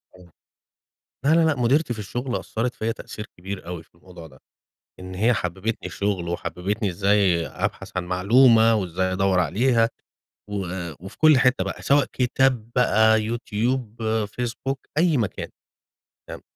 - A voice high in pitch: No, low, 110 Hz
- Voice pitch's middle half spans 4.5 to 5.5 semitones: Yes, average, 4.9 semitones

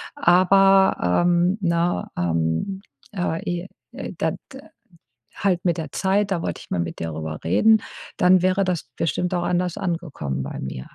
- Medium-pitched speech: Yes, medium, 175 Hz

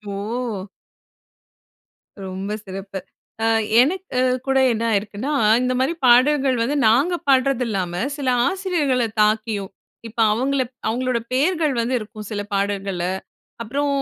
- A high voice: Yes, high, 240 Hz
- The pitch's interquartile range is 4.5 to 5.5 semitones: Yes, average, 4.8 semitones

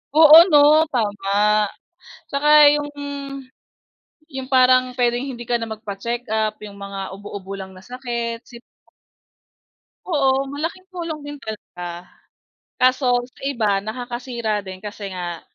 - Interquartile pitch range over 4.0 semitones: Yes, average, 4.4 semitones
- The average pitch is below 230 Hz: No, high, 235 Hz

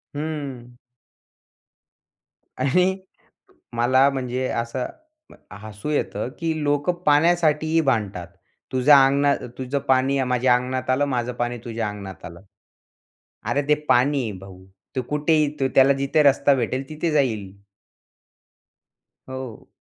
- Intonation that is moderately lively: Yes, average, 3.1 semitones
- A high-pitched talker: No, low, 130 Hz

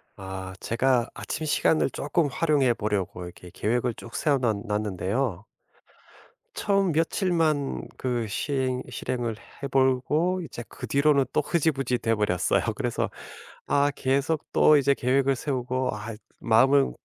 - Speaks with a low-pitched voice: Yes, low, 130 Hz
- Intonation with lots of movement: No, average, 4.1 semitones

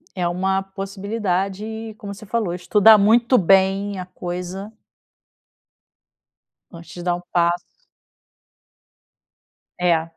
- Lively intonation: No, narrow, 2.6 semitones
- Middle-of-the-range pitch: No, high, 195 Hz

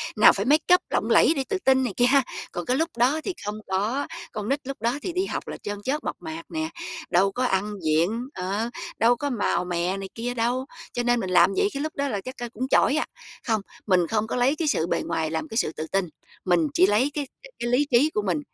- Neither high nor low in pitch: No, high, 230 Hz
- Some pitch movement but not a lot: No, wide, 5.7 semitones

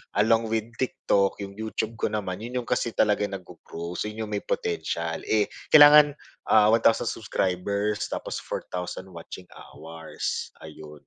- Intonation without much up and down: No, average, 3.8 semitones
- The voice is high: No, low, 105 Hz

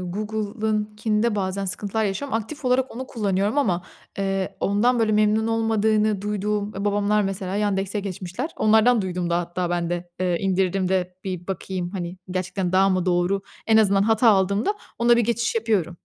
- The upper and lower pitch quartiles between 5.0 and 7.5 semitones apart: No, average, 2.8 semitones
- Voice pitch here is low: No, high, 200 Hz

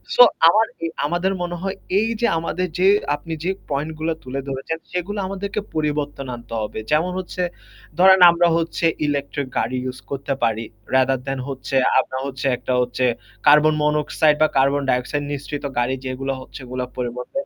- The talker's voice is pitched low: No, medium, 145 Hz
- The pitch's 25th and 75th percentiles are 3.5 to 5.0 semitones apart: Yes, average, 4.4 semitones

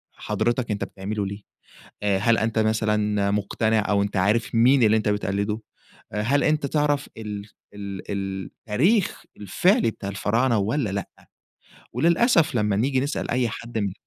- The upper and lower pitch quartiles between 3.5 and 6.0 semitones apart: Yes, average, 3.9 semitones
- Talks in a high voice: No, low, 110 Hz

